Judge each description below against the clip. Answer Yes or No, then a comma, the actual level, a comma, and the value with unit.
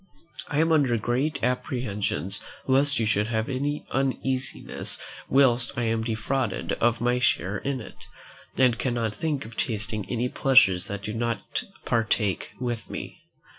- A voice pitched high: No, low, 120 Hz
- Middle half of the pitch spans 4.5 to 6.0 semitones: No, average, 3.3 semitones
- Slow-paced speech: No, average, 150 wpm